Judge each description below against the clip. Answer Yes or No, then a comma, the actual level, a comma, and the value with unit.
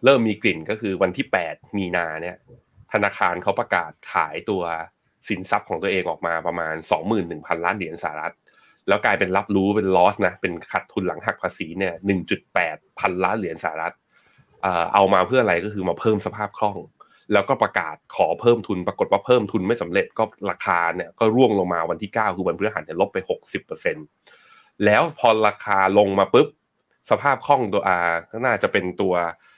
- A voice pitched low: Yes, low, 100 Hz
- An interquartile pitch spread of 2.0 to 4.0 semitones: No, average, 4.7 semitones